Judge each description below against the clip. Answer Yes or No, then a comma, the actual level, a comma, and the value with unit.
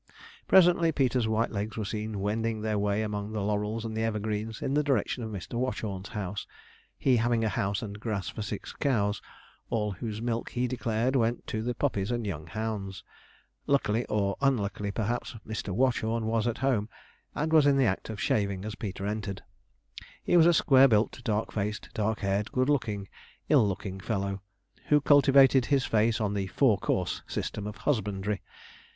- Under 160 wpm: No, average, 180 wpm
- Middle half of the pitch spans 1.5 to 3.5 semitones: Yes, average, 3.0 semitones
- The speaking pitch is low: Yes, low, 110 Hz